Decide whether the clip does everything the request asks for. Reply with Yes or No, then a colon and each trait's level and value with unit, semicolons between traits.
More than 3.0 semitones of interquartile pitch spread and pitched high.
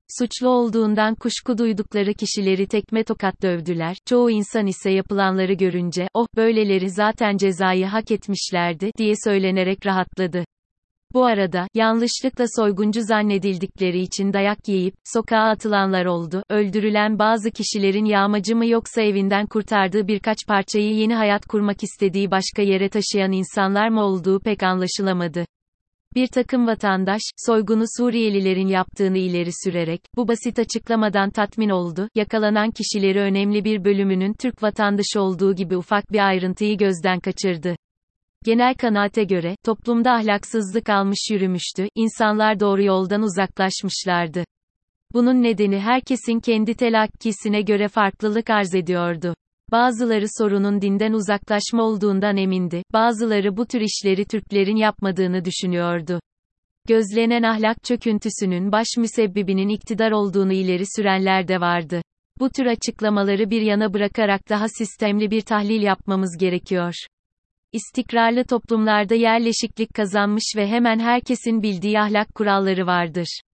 No: narrow, 2.6 semitones; high, 210 Hz